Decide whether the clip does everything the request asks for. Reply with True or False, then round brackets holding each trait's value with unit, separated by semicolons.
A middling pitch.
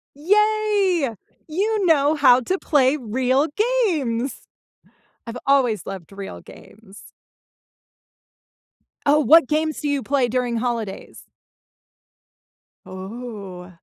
False (260 Hz)